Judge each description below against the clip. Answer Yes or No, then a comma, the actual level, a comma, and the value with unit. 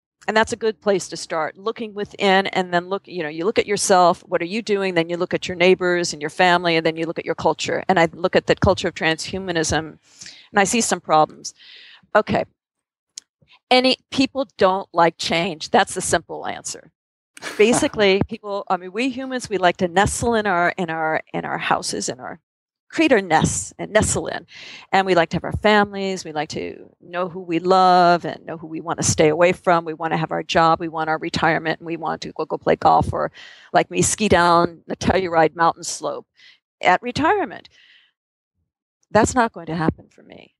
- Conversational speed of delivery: No, fast, 215 wpm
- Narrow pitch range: No, average, 3.3 semitones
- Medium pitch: Yes, medium, 180 Hz